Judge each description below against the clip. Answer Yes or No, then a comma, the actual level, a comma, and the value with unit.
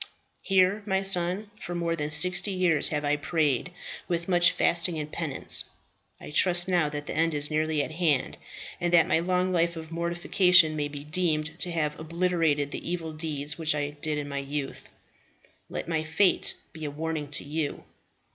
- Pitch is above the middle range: No, medium, 160 Hz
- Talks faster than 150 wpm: Yes, average, 185 wpm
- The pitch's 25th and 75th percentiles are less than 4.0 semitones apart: Yes, average, 2.8 semitones